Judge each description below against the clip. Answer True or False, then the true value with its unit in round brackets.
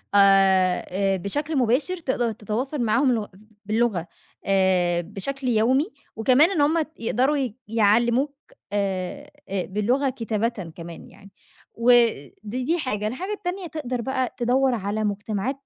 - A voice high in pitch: True (235 Hz)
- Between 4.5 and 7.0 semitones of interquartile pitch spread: True (5.0 semitones)